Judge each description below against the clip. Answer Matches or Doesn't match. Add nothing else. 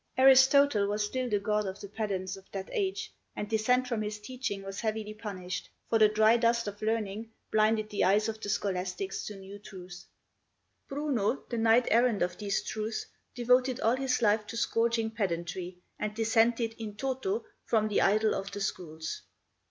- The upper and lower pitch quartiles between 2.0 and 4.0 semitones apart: Matches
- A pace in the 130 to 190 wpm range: Matches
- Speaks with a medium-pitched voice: Doesn't match